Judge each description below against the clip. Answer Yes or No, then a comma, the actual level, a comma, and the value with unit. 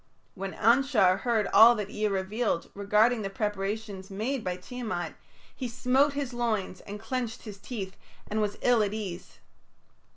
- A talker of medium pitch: No, high, 215 Hz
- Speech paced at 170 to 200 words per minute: No, average, 155 wpm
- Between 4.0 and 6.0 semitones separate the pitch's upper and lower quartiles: No, average, 3.5 semitones